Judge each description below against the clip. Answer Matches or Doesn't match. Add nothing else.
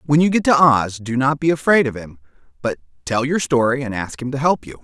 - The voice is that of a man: Matches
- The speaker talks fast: Matches